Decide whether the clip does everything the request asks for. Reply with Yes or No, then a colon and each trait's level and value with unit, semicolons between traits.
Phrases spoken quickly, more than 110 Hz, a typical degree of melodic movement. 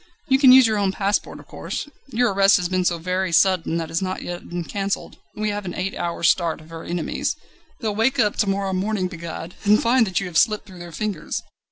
Yes: fast, 245 wpm; high, 190 Hz; average, 3.3 semitones